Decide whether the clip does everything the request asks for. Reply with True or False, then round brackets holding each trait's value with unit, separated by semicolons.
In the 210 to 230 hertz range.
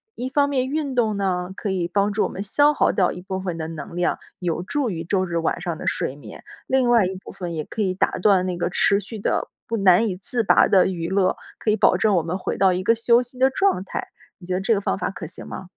False (190 Hz)